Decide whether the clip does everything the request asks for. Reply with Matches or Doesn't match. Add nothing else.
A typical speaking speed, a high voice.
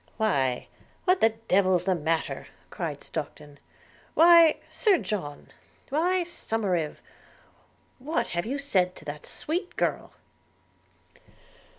Doesn't match